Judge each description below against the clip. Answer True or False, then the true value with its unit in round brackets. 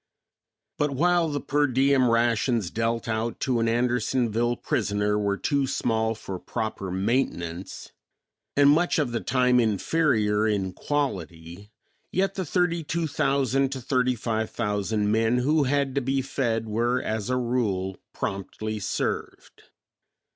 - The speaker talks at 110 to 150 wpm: True (140 wpm)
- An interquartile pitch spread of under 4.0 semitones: False (4.3 semitones)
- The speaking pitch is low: True (120 Hz)